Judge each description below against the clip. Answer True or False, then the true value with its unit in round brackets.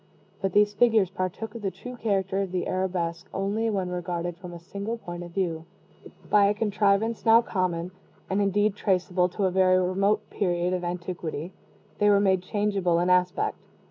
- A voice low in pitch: False (190 Hz)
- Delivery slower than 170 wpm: False (175 wpm)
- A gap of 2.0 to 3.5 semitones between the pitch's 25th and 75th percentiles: True (2.4 semitones)